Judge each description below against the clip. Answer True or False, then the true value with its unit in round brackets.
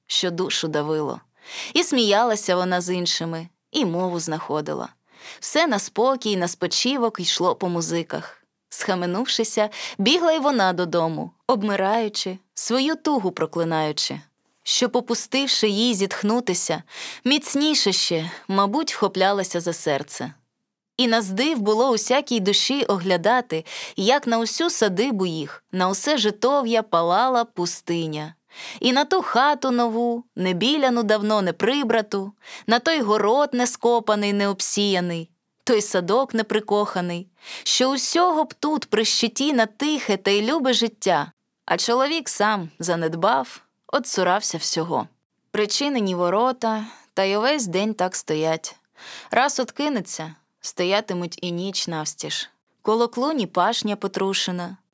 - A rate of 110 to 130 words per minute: True (120 wpm)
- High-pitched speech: True (210 Hz)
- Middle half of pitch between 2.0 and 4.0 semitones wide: False (5.4 semitones)